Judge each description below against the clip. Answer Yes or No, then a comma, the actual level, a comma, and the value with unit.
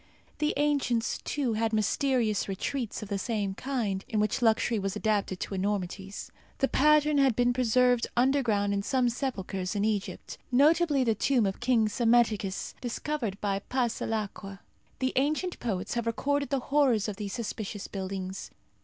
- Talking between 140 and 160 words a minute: Yes, average, 155 wpm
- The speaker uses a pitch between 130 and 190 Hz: No, high, 225 Hz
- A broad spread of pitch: No, average, 4.5 semitones